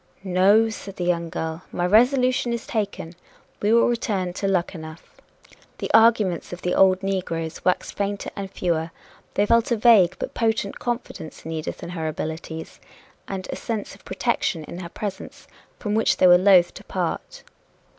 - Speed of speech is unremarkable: Yes, average, 170 wpm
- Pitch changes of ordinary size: Yes, average, 4.1 semitones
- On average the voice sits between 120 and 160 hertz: No, high, 190 Hz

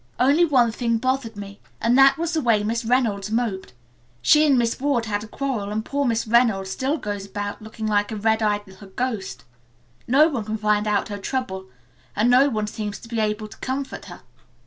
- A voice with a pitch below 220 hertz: No, high, 225 Hz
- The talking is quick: Yes, fast, 210 wpm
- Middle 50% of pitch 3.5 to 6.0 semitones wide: Yes, average, 3.8 semitones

